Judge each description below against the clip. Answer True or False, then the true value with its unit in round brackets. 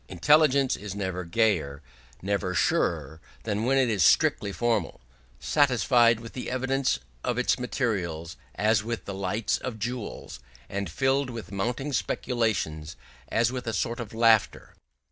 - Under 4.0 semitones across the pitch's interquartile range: False (4.4 semitones)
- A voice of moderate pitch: False (115 Hz)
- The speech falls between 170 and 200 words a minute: False (145 wpm)